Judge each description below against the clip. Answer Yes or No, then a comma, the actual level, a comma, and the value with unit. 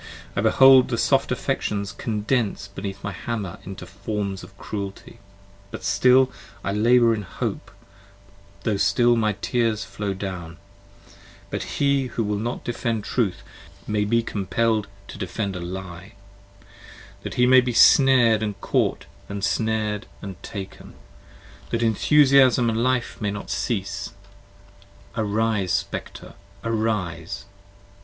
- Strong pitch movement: No, average, 2.9 semitones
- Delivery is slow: Yes, slow, 130 wpm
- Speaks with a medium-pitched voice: No, low, 105 Hz